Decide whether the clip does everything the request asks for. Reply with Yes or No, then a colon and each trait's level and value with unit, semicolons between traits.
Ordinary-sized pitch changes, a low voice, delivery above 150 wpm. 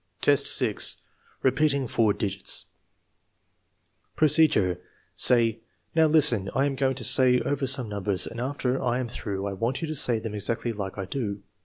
Yes: average, 4.9 semitones; low, 120 Hz; average, 165 wpm